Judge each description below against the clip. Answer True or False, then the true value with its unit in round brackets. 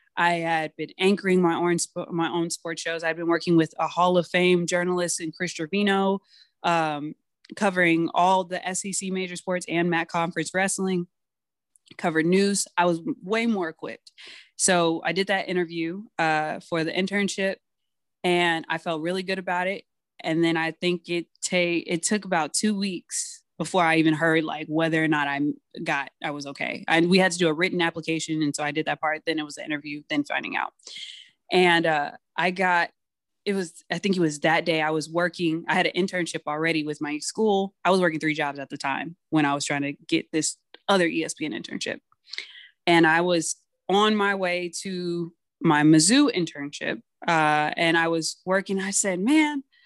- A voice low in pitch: False (170 Hz)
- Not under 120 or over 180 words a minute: False (195 wpm)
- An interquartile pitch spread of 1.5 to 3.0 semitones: True (2.7 semitones)